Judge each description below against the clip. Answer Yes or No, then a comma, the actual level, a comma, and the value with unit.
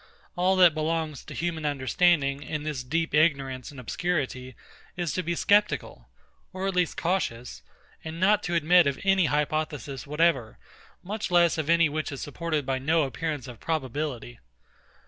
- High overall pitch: No, medium, 155 Hz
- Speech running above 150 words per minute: Yes, average, 160 wpm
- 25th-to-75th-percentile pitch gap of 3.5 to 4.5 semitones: Yes, average, 3.9 semitones